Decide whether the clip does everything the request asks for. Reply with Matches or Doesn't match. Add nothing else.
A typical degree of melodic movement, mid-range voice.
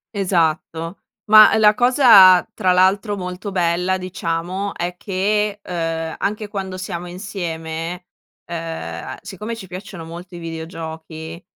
Matches